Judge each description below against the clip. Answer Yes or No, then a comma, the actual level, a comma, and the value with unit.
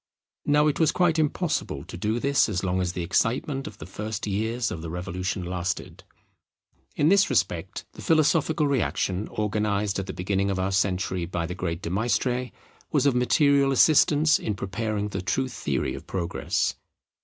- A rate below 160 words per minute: No, average, 175 wpm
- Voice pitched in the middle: No, low, 105 Hz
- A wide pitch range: Yes, wide, 6.7 semitones